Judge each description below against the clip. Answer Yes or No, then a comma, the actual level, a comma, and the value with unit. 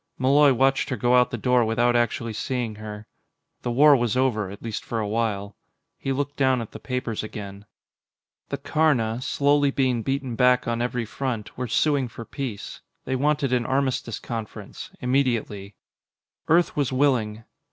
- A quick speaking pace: No, average, 165 wpm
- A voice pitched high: No, low, 125 Hz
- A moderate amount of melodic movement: Yes, average, 3.2 semitones